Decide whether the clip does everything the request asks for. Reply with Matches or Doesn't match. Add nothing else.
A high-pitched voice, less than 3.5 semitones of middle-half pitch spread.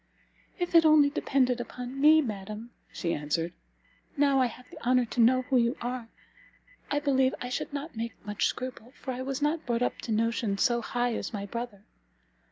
Matches